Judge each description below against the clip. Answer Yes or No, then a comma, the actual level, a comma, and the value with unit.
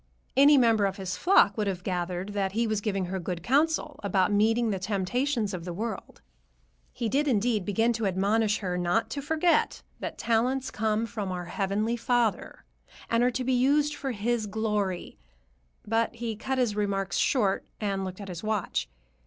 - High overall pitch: Yes, high, 215 Hz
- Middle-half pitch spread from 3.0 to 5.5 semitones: Yes, average, 3.6 semitones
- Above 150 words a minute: Yes, average, 180 wpm